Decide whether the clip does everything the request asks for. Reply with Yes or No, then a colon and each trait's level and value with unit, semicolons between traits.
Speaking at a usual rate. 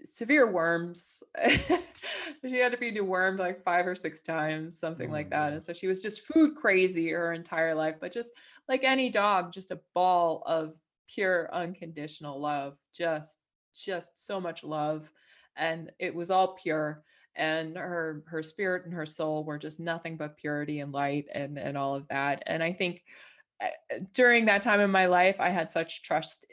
Yes: average, 180 wpm